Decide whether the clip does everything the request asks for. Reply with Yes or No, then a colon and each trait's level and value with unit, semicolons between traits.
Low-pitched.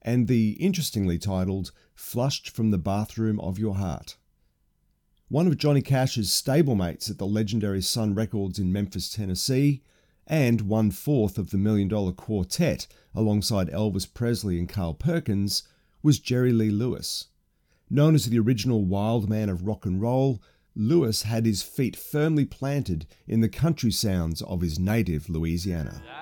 Yes: low, 105 Hz